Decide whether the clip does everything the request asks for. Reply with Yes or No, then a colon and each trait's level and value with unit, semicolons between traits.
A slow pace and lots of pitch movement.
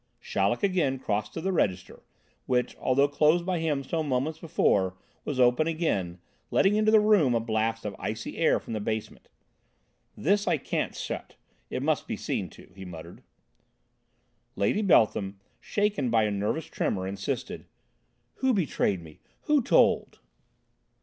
No: average, 155 wpm; wide, 8.7 semitones